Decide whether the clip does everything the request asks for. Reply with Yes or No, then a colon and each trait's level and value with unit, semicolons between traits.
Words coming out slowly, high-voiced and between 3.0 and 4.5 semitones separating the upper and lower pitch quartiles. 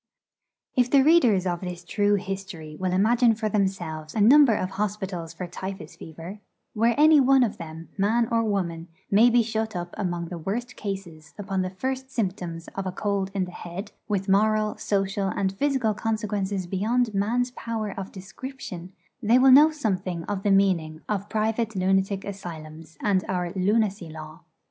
No: average, 170 wpm; high, 195 Hz; average, 3.5 semitones